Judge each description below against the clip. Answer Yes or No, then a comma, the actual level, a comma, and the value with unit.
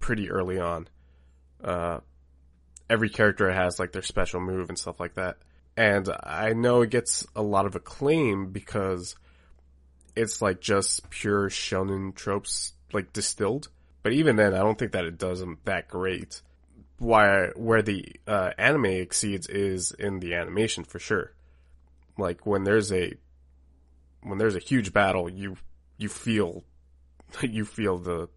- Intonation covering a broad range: Yes, wide, 7.0 semitones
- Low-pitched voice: Yes, very low, 90 Hz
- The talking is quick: No, average, 150 wpm